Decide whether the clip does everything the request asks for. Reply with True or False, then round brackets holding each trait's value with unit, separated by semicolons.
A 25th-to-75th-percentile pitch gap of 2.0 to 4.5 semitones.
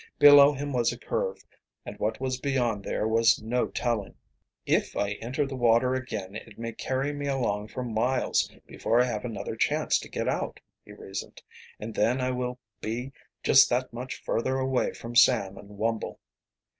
True (2.7 semitones)